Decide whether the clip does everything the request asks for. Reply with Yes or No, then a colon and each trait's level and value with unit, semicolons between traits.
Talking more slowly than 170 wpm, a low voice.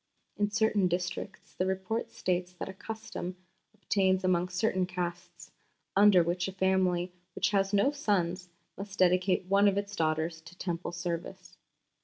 No: average, 150 wpm; medium, 185 Hz